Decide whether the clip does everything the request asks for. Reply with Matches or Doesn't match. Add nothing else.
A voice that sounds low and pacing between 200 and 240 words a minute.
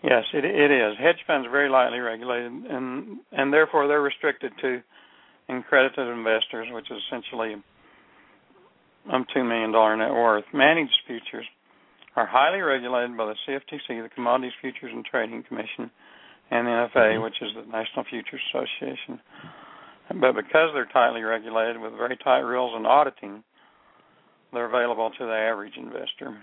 Doesn't match